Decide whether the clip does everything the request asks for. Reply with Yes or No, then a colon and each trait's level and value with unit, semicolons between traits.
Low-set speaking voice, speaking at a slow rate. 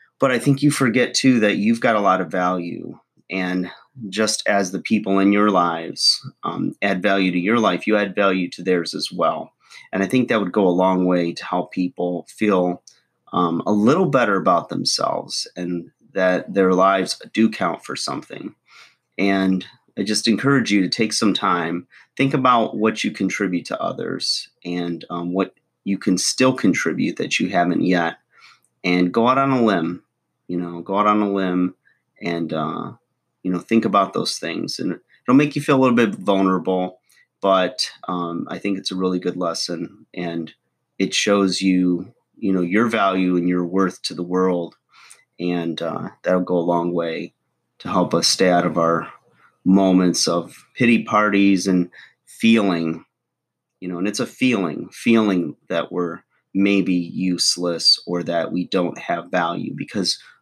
No: very low, 95 Hz; average, 180 wpm